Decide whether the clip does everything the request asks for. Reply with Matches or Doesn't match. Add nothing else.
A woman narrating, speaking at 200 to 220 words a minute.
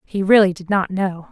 Doesn't match